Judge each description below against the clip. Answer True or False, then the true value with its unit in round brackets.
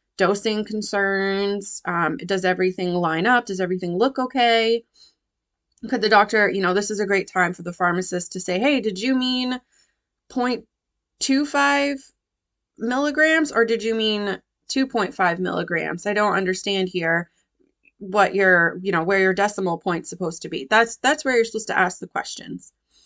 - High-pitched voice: True (205 Hz)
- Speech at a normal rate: True (165 wpm)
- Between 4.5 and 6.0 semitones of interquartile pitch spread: True (5.1 semitones)